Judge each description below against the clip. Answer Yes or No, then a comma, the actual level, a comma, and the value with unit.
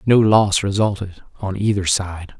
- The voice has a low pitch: Yes, low, 100 Hz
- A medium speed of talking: Yes, average, 150 wpm